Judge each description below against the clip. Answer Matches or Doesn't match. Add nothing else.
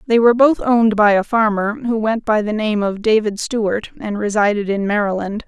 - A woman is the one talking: Matches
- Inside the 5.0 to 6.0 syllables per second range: Matches